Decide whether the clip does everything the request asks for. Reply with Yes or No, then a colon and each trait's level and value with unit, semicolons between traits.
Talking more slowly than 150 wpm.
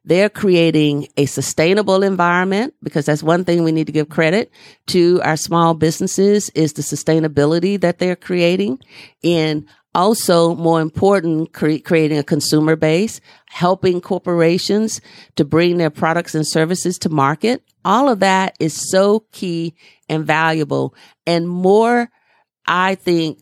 Yes: average, 140 wpm